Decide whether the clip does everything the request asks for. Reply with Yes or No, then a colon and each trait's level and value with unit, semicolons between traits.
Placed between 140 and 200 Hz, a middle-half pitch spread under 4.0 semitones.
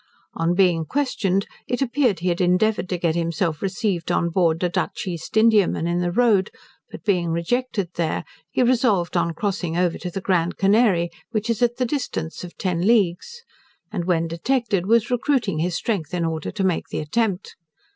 No: medium, 185 Hz; average, 4.8 semitones